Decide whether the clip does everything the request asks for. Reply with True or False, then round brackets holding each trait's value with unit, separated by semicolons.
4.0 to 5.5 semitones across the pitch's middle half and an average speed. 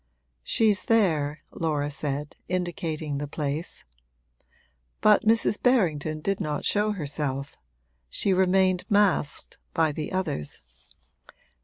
False (4.8 semitones; 105 wpm)